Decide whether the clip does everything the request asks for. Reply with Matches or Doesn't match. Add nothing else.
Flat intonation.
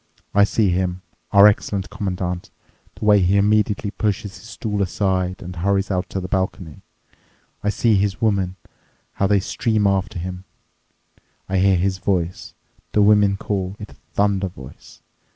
Matches